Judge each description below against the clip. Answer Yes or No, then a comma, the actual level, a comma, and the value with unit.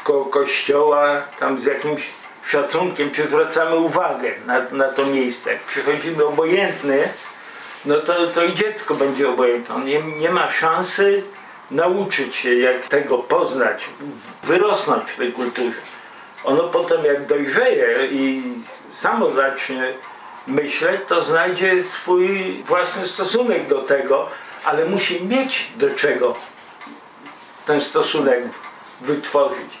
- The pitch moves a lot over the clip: Yes, wide, 6.0 semitones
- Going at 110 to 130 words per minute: Yes, average, 120 wpm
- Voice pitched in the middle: Yes, medium, 165 Hz